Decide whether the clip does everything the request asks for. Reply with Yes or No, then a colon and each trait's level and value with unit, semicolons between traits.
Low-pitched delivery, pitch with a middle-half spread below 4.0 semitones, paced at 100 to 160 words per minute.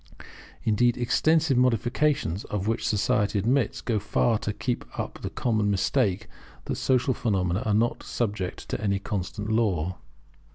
Yes: low, 110 Hz; average, 3.3 semitones; average, 150 wpm